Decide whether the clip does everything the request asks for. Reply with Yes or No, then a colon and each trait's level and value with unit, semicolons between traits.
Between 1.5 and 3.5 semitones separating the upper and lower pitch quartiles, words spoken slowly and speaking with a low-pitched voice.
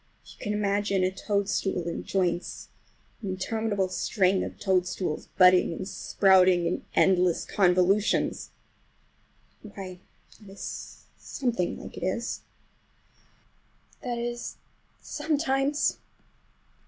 No: average, 2.8 semitones; slow, 95 wpm; high, 195 Hz